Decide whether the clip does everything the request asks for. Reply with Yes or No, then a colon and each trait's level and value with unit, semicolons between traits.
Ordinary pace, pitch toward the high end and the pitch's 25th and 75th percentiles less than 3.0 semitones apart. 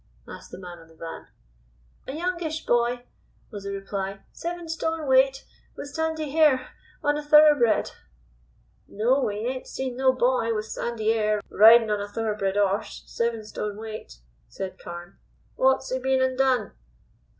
No: average, 155 wpm; high, 240 Hz; average, 4.5 semitones